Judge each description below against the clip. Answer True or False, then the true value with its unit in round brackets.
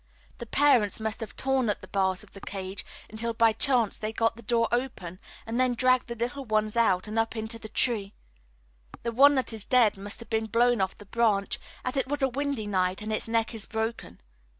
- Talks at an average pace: False (220 wpm)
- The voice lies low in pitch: False (225 Hz)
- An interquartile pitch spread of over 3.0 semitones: False (2.6 semitones)